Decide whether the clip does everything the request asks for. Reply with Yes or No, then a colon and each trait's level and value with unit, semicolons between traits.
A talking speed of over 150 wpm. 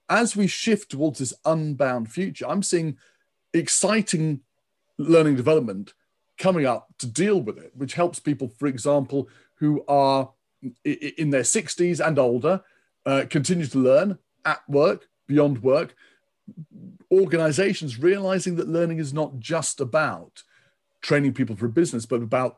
No: average, 140 wpm